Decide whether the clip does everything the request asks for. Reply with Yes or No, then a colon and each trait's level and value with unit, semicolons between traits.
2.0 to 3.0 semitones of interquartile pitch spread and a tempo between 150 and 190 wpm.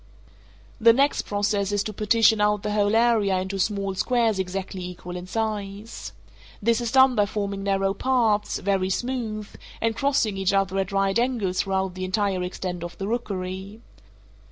Yes: average, 2.7 semitones; average, 165 wpm